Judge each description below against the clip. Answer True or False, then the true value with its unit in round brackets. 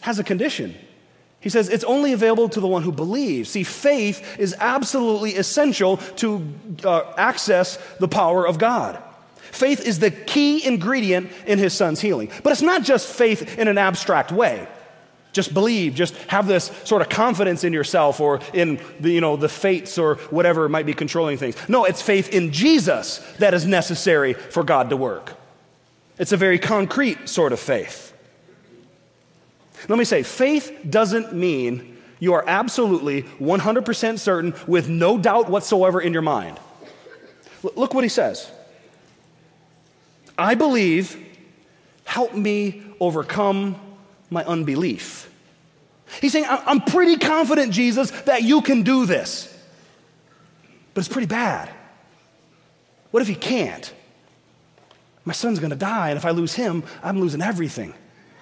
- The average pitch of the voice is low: False (195 Hz)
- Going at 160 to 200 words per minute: False (150 wpm)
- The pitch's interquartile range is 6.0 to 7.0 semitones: False (5.5 semitones)